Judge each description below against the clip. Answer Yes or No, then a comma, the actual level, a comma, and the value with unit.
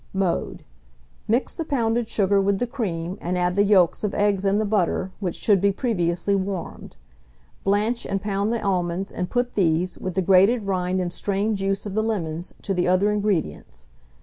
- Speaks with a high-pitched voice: Yes, high, 195 Hz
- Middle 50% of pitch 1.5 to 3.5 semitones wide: Yes, narrow, 2.6 semitones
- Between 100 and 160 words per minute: No, average, 185 wpm